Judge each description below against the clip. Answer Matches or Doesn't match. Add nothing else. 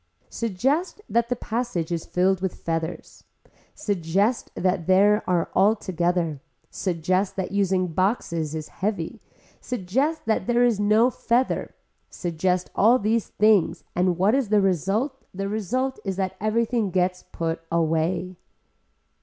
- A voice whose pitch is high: Matches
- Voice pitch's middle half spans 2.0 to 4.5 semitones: Matches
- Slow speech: Matches